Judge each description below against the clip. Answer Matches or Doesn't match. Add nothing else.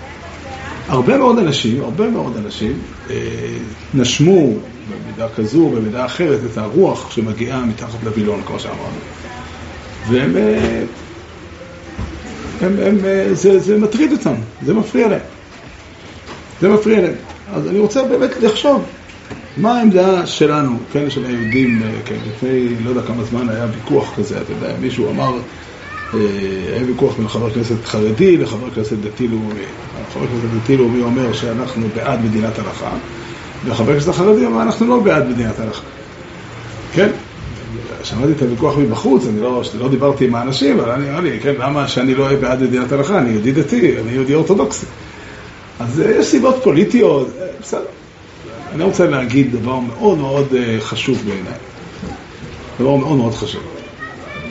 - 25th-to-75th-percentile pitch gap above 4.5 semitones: Matches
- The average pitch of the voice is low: Matches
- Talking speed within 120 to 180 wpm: Matches